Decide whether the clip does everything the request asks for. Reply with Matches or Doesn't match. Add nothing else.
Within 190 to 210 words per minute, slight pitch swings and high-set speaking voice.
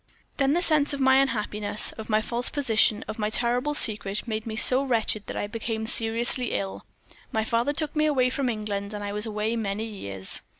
Doesn't match